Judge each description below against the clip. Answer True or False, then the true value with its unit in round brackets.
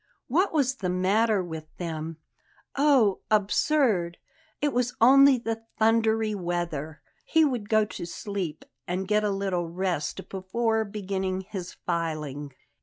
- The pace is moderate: False (130 wpm)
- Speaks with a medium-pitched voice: False (200 Hz)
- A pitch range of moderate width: True (4.5 semitones)